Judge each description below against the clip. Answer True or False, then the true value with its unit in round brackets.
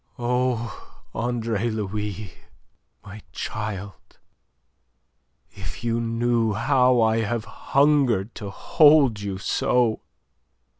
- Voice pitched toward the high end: False (115 Hz)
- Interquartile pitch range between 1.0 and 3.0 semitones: True (2.6 semitones)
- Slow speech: True (90 wpm)